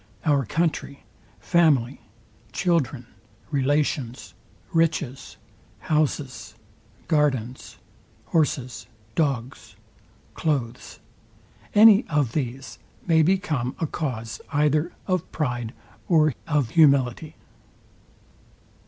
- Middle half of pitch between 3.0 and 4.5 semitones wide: Yes, average, 4.1 semitones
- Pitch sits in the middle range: Yes, medium, 145 Hz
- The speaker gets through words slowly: Yes, slow, 75 wpm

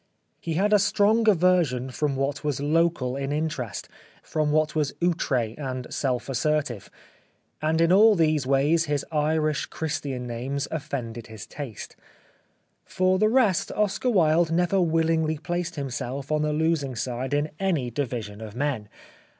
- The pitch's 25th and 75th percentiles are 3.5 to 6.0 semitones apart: Yes, average, 4.0 semitones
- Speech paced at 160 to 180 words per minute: No, average, 150 wpm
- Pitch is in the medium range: Yes, medium, 150 Hz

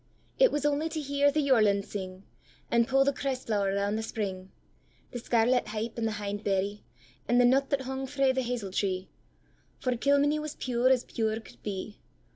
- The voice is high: Yes, high, 235 Hz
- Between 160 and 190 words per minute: Yes, average, 170 wpm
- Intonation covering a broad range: No, average, 4.9 semitones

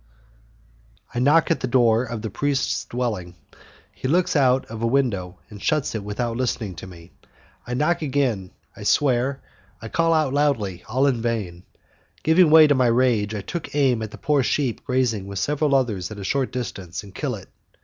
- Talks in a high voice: No, low, 125 Hz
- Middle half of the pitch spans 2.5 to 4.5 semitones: No, average, 4.9 semitones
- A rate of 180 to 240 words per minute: Yes, average, 190 wpm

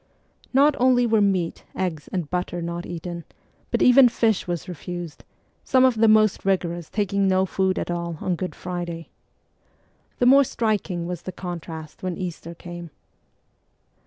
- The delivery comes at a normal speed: Yes, average, 155 wpm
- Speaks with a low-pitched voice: No, medium, 180 Hz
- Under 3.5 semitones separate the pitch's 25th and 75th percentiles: No, average, 3.8 semitones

